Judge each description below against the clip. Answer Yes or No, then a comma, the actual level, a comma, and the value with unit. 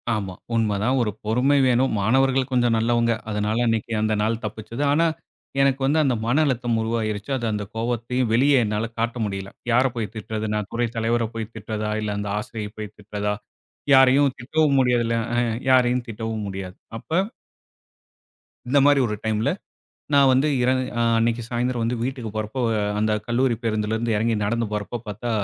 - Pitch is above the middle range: No, low, 115 Hz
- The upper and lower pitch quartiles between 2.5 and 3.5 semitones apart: Yes, average, 2.8 semitones